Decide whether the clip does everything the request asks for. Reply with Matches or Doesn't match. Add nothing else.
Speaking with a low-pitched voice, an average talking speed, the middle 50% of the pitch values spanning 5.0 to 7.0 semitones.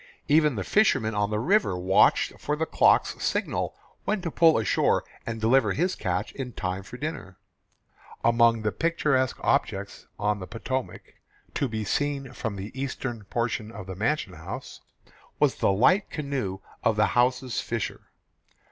Matches